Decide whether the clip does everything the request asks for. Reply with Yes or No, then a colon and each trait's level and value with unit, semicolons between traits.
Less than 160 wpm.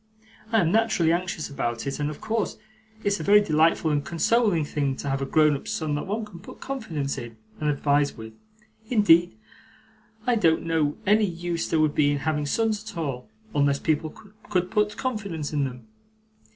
No: average, 190 wpm